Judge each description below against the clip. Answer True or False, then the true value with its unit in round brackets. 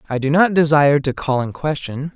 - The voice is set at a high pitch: False (145 Hz)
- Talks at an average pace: False (225 wpm)